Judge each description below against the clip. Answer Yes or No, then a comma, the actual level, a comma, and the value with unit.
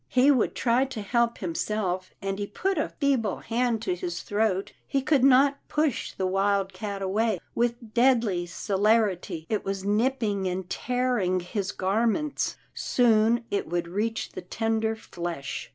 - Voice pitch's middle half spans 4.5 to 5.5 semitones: No, average, 4.0 semitones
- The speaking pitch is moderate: No, high, 215 Hz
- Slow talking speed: No, average, 150 wpm